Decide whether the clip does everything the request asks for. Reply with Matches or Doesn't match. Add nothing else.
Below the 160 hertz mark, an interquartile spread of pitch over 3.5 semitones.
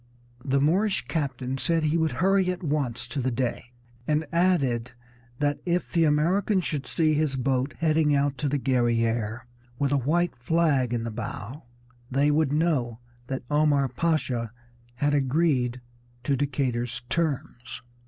Matches